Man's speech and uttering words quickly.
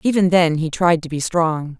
No: female; fast, 235 wpm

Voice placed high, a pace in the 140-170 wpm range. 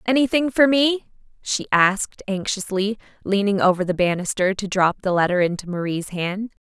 Yes: high, 200 Hz; average, 155 wpm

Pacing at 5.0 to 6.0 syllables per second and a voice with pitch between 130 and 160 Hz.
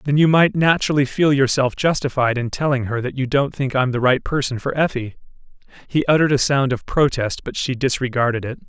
Yes: 5.8 syllables/s; low, 135 Hz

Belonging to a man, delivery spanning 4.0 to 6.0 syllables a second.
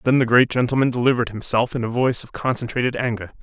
No: male; 7.1 syllables/s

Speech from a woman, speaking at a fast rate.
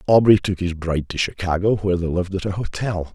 No: male; fast, 230 wpm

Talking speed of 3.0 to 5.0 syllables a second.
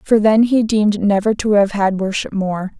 Yes: 4.8 syllables/s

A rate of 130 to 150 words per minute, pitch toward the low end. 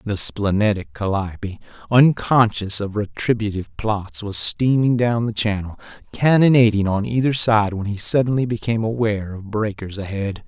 Yes: slow, 135 wpm; low, 105 Hz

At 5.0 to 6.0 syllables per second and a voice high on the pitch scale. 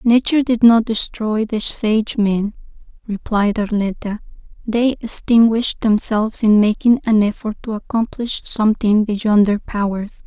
No: 4.5 syllables/s; high, 215 Hz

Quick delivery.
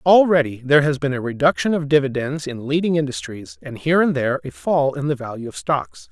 Yes: fast, 215 wpm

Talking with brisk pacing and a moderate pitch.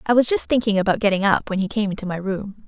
No: fast, 290 wpm; high, 205 Hz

